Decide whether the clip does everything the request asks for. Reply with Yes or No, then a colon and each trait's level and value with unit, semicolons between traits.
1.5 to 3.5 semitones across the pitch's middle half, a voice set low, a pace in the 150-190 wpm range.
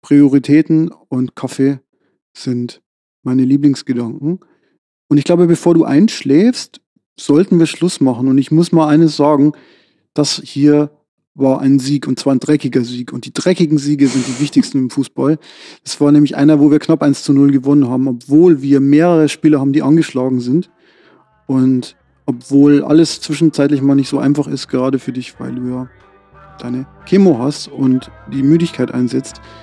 No: average, 2.7 semitones; medium, 145 Hz; average, 170 wpm